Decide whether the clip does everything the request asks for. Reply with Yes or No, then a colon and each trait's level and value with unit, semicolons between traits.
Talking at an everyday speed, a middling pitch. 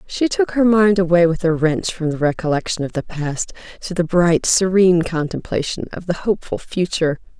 Yes: average, 185 wpm; medium, 175 Hz